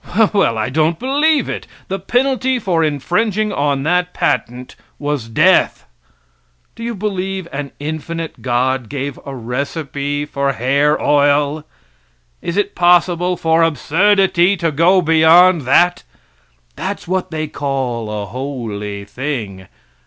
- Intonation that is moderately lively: Yes, average, 5.0 semitones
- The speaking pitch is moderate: Yes, medium, 155 Hz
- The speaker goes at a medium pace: No, slow, 125 wpm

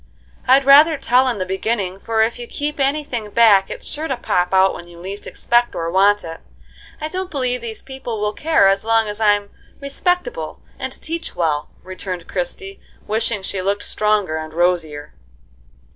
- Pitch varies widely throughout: Yes, wide, 6.0 semitones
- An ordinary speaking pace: Yes, average, 180 wpm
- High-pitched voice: Yes, high, 215 Hz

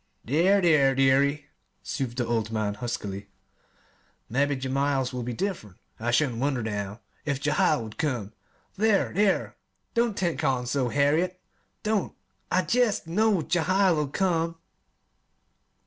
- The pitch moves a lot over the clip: Yes, wide, 6.5 semitones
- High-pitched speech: No, medium, 140 Hz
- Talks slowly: Yes, slow, 130 wpm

